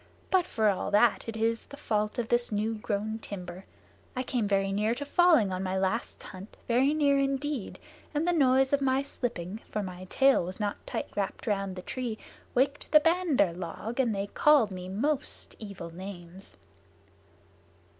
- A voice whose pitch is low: No, high, 220 Hz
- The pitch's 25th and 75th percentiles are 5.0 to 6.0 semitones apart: Yes, wide, 5.5 semitones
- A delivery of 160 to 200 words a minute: Yes, average, 175 wpm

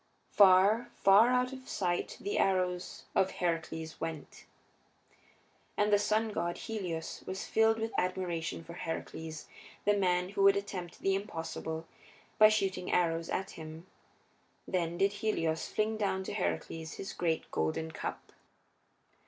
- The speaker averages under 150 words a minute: Yes, slow, 135 wpm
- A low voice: No, medium, 185 Hz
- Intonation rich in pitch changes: No, average, 3.7 semitones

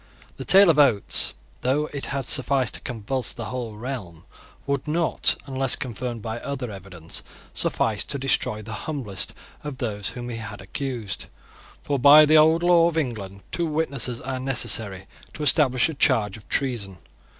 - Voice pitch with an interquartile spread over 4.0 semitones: Yes, average, 4.7 semitones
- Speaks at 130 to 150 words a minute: No, average, 165 wpm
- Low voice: Yes, low, 130 Hz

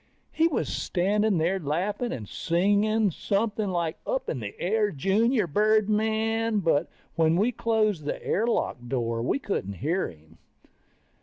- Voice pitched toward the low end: No, high, 200 Hz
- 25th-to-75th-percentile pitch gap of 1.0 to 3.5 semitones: No, average, 5.3 semitones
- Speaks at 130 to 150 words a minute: Yes, average, 145 wpm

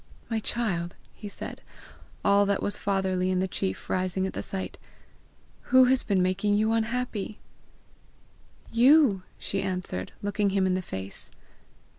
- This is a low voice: No, high, 195 Hz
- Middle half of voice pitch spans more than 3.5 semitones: No, average, 2.9 semitones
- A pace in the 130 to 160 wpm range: Yes, average, 145 wpm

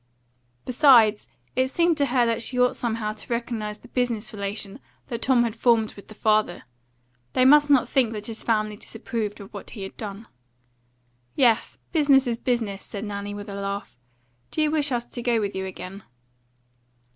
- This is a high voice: Yes, high, 225 Hz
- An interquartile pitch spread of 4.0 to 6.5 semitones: No, average, 3.3 semitones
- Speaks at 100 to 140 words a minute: No, average, 180 wpm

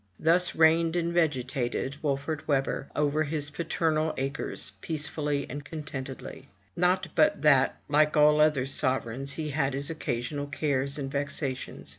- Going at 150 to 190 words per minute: No, slow, 135 wpm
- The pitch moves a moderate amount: No, narrow, 2.3 semitones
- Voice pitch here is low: No, medium, 145 Hz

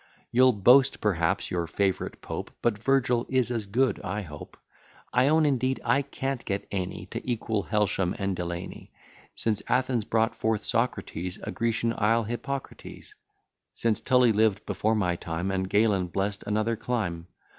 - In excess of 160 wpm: No, average, 155 wpm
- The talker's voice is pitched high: No, low, 110 Hz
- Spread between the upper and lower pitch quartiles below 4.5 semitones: Yes, average, 4.1 semitones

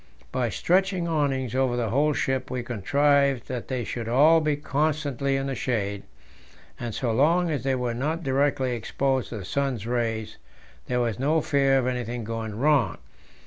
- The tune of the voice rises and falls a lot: No, average, 3.3 semitones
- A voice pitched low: Yes, low, 130 Hz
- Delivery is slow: No, average, 175 wpm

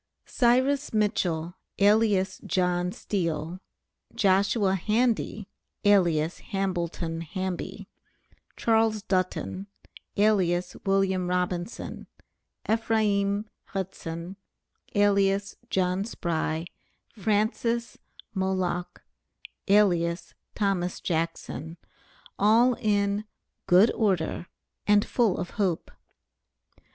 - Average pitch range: Yes, average, 3.0 semitones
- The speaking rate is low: Yes, slow, 75 wpm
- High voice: Yes, high, 195 Hz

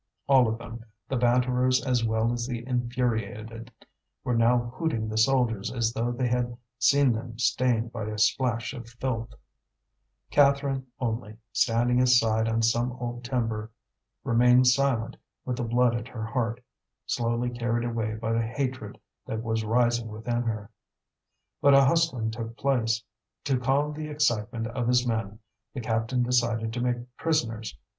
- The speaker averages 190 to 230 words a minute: No, average, 155 wpm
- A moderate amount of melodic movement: No, narrow, 1.8 semitones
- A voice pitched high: No, low, 120 Hz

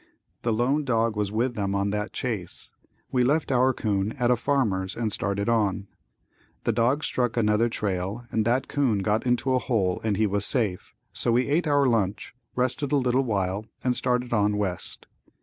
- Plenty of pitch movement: No, average, 3.7 semitones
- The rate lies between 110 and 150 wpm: No, average, 185 wpm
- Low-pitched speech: Yes, low, 115 Hz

